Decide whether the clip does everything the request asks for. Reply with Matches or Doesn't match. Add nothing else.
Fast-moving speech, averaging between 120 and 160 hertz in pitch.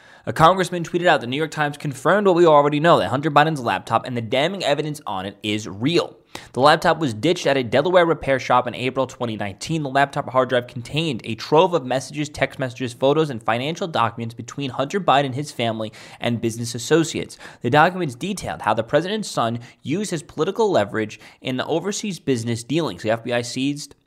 Doesn't match